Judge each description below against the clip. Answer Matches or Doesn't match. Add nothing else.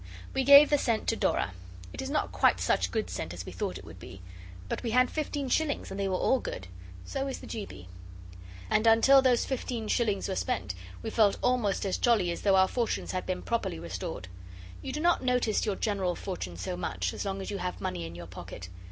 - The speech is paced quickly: Matches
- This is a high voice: Matches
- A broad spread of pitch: Matches